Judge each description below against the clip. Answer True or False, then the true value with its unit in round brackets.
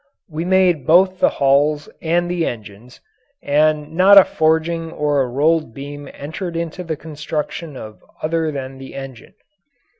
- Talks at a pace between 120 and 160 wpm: True (150 wpm)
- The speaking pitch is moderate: True (155 Hz)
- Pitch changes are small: False (3.1 semitones)